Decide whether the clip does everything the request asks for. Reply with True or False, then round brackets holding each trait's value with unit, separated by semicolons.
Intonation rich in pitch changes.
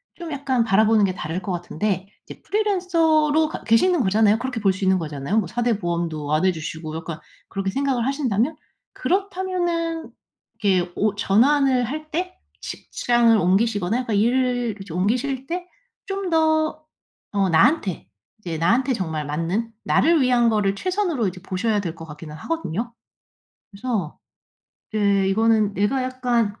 True (6.8 semitones)